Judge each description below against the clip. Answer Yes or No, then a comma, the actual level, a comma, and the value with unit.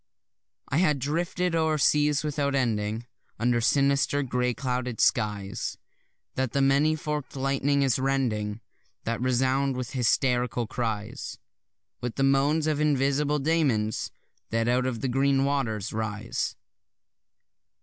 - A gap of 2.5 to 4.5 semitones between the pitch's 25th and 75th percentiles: Yes, average, 3.1 semitones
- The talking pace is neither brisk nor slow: No, slow, 125 wpm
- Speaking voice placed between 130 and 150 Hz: Yes, low, 135 Hz